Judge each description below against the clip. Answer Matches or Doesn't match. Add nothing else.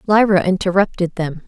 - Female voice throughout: Matches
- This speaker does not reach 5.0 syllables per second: Doesn't match